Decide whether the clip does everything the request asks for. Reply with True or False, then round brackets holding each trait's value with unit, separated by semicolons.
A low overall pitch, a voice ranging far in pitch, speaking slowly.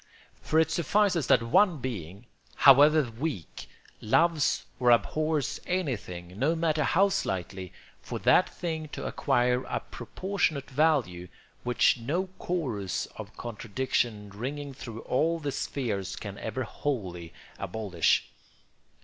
True (130 Hz; 7.0 semitones; 120 wpm)